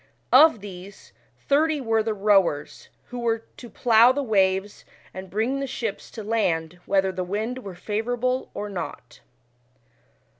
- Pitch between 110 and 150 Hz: No, high, 215 Hz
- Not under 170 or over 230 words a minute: No, average, 145 wpm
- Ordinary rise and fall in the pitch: Yes, average, 4.2 semitones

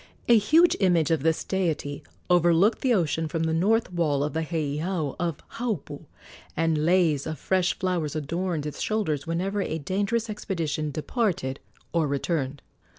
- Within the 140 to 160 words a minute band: Yes, average, 150 wpm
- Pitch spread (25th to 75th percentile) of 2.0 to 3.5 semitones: No, average, 3.9 semitones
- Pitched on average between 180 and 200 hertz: No, medium, 165 Hz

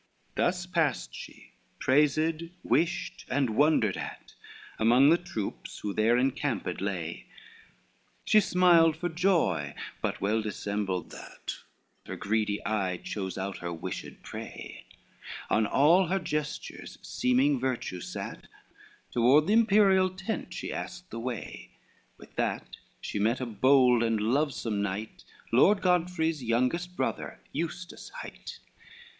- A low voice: Yes, low, 130 Hz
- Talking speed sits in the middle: No, slow, 125 wpm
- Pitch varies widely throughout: Yes, wide, 8.0 semitones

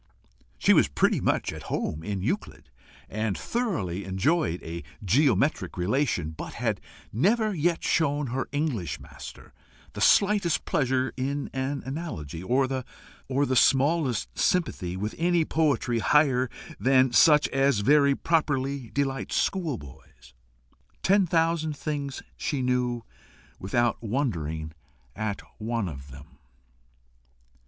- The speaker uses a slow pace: Yes, slow, 115 wpm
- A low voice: Yes, low, 130 Hz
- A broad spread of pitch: Yes, wide, 6.8 semitones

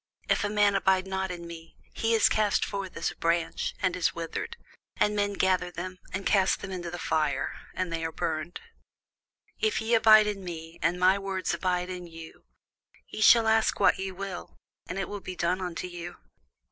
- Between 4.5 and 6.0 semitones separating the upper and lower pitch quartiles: No, average, 2.7 semitones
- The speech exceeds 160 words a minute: Yes, average, 195 wpm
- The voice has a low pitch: No, medium, 185 Hz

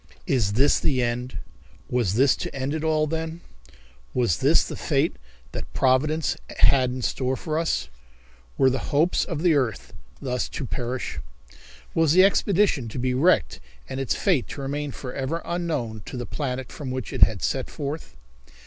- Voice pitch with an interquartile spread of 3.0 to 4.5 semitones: Yes, average, 3.8 semitones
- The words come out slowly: No, average, 170 wpm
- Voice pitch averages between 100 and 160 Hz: Yes, low, 135 Hz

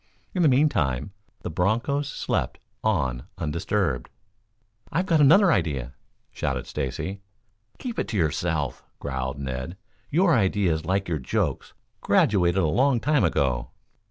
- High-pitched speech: No, very low, 90 Hz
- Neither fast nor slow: No, slow, 130 wpm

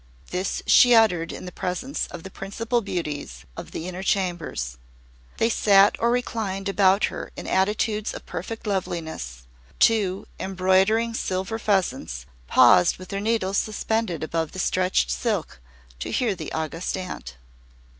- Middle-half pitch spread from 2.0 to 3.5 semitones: No, average, 4.2 semitones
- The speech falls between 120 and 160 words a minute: Yes, average, 145 wpm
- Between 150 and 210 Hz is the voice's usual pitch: Yes, high, 190 Hz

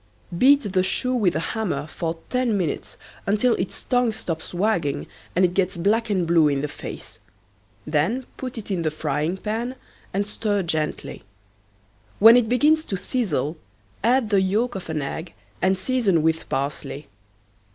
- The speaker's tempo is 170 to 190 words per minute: No, average, 160 wpm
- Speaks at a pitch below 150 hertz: No, high, 190 Hz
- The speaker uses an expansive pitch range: Yes, wide, 5.9 semitones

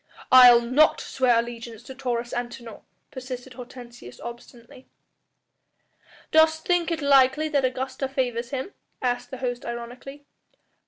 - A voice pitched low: No, very high, 255 Hz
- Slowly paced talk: Yes, slow, 125 wpm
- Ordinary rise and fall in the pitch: No, narrow, 2.2 semitones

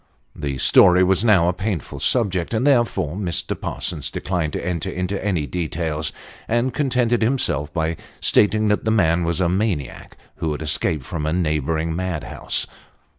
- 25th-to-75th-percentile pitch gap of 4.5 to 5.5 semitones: Yes, average, 4.9 semitones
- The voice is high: No, very low, 90 Hz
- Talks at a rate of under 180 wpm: Yes, average, 165 wpm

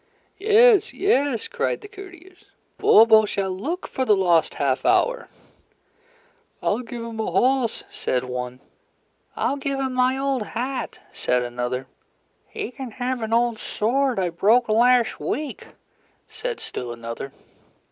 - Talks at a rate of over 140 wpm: No, slow, 135 wpm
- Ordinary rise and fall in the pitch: No, wide, 6.4 semitones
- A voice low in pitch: No, high, 240 Hz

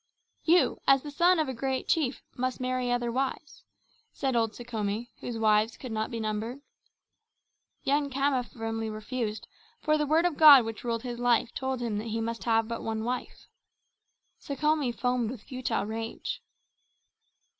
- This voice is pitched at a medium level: No, high, 245 Hz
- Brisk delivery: No, average, 165 wpm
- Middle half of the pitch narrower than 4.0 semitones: Yes, average, 3.2 semitones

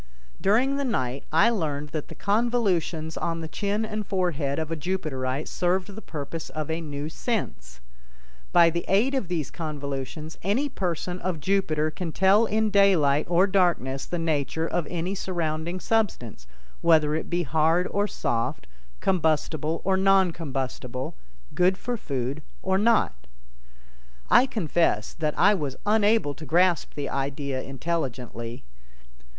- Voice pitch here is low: No, medium, 165 Hz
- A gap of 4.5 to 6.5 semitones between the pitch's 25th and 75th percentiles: Yes, average, 4.8 semitones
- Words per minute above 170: No, average, 145 wpm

